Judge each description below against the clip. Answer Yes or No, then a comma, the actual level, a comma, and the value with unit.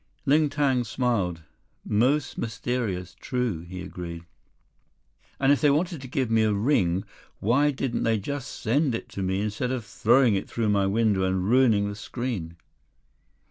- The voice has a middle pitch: No, low, 115 Hz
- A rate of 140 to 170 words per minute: Yes, average, 160 wpm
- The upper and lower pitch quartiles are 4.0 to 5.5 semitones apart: Yes, average, 5.2 semitones